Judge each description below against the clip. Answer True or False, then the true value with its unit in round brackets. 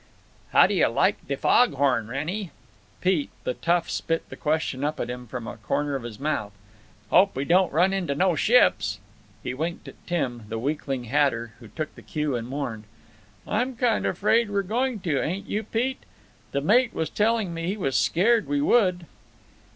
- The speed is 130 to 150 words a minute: False (190 wpm)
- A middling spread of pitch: False (7.2 semitones)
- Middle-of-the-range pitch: True (165 Hz)